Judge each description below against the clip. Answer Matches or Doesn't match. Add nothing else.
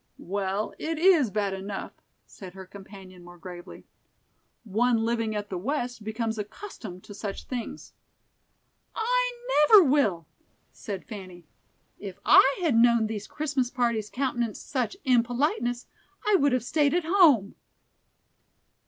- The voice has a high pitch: Matches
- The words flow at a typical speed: Doesn't match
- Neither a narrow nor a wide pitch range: Doesn't match